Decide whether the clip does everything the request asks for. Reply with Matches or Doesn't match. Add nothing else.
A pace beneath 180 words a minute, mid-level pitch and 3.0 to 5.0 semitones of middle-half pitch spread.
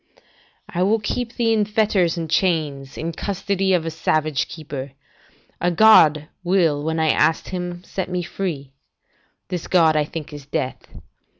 Matches